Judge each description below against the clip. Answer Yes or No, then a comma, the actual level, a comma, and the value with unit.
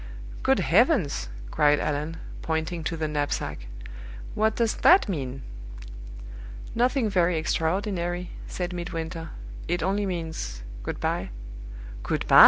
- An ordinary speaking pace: No, slow, 115 wpm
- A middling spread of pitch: Yes, average, 3.5 semitones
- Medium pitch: Yes, medium, 165 Hz